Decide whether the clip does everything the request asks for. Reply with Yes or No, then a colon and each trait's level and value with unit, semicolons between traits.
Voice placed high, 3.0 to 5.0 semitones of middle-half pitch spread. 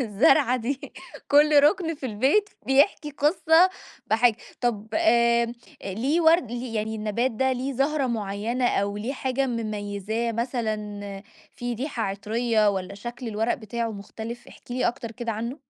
Yes: high, 235 Hz; average, 3.7 semitones